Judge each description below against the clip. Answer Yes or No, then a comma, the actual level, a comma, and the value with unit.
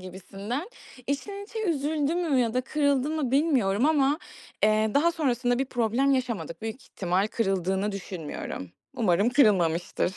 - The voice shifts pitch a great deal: Yes, wide, 6.6 semitones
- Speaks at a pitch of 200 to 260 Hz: Yes, high, 245 Hz